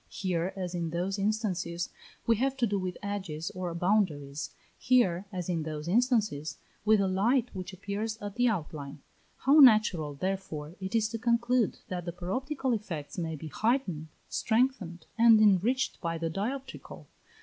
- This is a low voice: No, high, 195 Hz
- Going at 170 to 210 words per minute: No, average, 160 wpm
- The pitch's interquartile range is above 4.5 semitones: Yes, average, 5.0 semitones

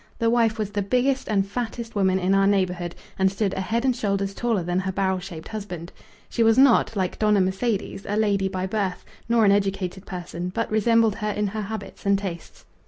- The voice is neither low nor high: No, high, 200 Hz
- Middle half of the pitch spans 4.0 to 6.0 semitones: No, narrow, 2.6 semitones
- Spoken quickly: Yes, fast, 210 wpm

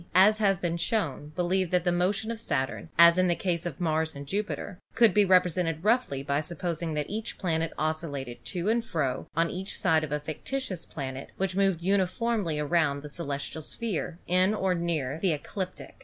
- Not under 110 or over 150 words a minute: No, average, 195 wpm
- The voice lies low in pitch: No, medium, 170 Hz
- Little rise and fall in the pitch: No, average, 3.6 semitones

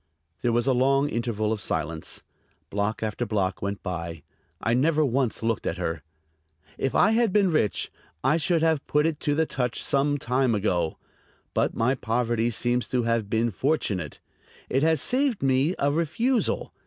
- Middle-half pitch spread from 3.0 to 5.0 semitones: No, wide, 5.5 semitones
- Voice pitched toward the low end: Yes, low, 125 Hz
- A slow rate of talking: No, average, 170 wpm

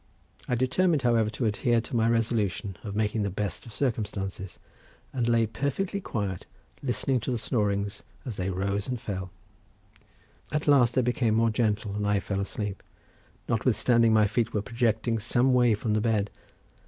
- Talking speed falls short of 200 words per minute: Yes, average, 165 wpm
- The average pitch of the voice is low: Yes, low, 110 Hz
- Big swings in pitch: No, average, 2.9 semitones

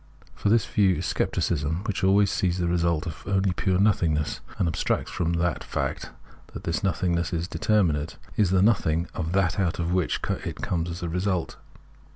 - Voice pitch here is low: Yes, very low, 90 Hz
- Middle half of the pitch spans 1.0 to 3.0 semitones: Yes, narrow, 2.5 semitones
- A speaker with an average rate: Yes, average, 185 wpm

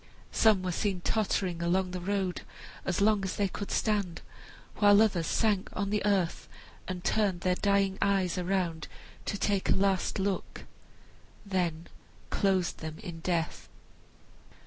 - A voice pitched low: No, high, 190 Hz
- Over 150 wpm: No, average, 145 wpm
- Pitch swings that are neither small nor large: No, narrow, 2.2 semitones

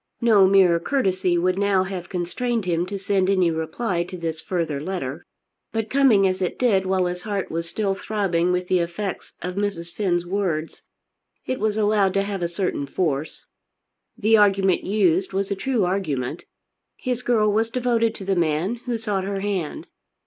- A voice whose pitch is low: No, high, 190 Hz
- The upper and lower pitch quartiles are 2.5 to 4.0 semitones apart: Yes, average, 3.0 semitones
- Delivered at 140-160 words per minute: No, average, 180 wpm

